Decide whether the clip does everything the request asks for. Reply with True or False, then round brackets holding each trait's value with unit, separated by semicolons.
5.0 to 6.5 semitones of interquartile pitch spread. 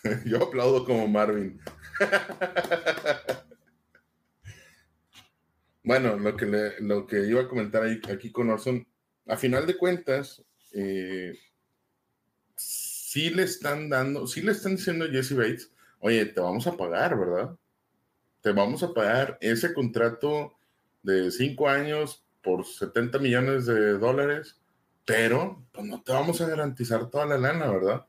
True (5.6 semitones)